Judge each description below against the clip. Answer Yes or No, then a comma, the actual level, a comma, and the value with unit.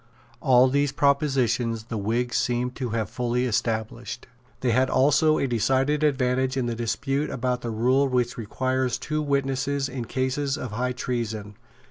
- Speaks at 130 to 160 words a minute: Yes, average, 155 wpm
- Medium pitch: No, low, 125 Hz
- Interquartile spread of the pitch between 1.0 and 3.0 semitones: Yes, narrow, 2.4 semitones